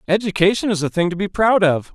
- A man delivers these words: Yes, male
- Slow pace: No, fast, 245 wpm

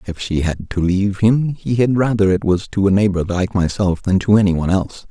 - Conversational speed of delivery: No, fast, 235 wpm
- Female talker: No, male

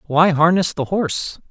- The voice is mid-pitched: Yes, medium, 165 Hz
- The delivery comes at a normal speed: Yes, average, 160 wpm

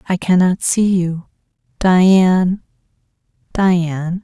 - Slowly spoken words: Yes, slow, 85 wpm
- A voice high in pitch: No, medium, 180 Hz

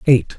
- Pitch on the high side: No, low, 135 Hz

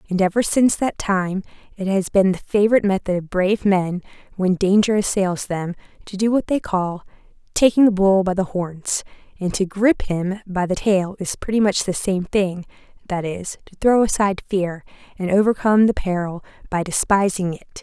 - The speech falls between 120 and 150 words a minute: No, average, 180 wpm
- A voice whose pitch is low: No, high, 195 Hz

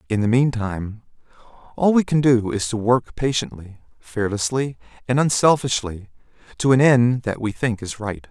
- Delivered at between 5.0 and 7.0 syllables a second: No, 4.8 syllables/s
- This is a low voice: Yes, low, 115 Hz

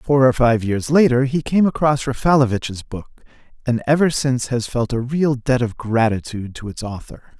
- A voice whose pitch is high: No, low, 125 Hz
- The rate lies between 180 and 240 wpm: Yes, average, 185 wpm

